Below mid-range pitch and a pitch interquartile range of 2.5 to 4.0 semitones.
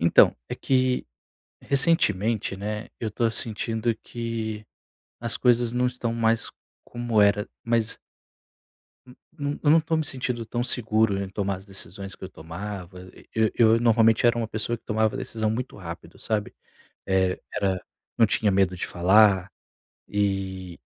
Yes: low, 110 Hz; average, 3.3 semitones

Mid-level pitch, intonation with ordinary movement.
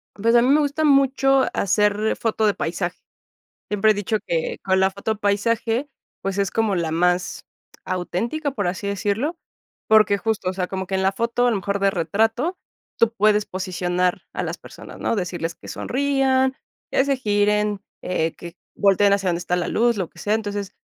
No: high, 205 Hz; average, 3.6 semitones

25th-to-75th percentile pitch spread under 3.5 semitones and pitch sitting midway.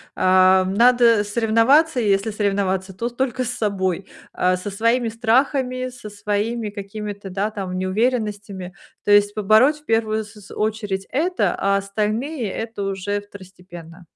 No: average, 3.0 semitones; high, 210 Hz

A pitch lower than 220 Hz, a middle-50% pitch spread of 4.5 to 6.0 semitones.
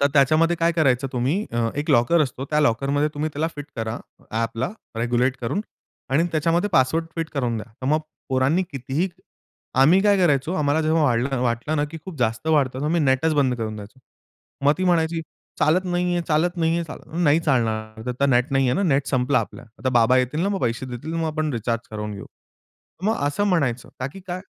Yes: medium, 140 Hz; average, 4.8 semitones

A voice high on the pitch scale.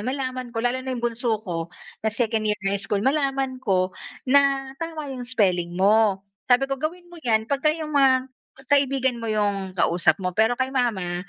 Yes: high, 245 Hz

